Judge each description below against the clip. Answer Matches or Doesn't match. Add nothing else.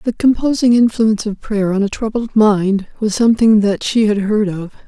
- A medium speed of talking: Matches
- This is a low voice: Doesn't match